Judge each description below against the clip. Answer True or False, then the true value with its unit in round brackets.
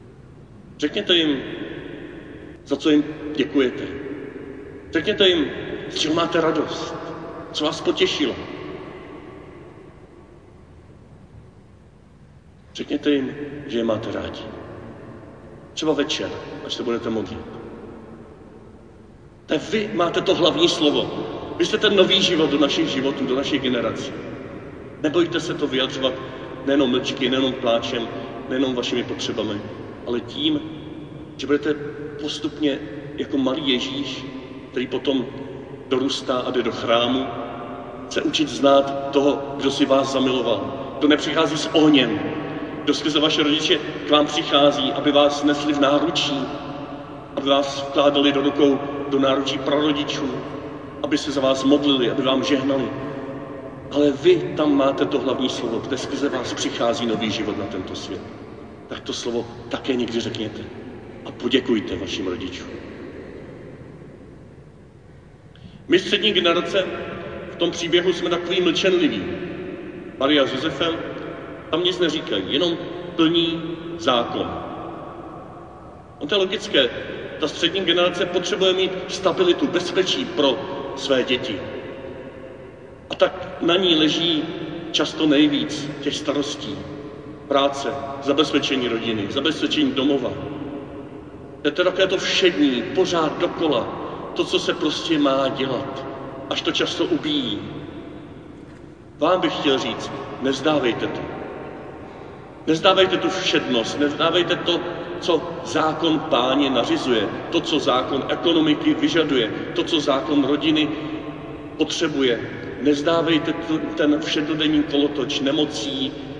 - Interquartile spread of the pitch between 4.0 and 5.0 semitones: False (3.6 semitones)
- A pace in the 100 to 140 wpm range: True (120 wpm)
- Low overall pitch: False (145 Hz)